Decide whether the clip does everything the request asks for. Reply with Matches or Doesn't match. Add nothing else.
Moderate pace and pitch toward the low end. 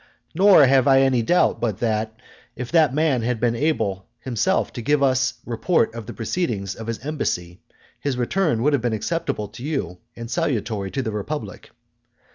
Matches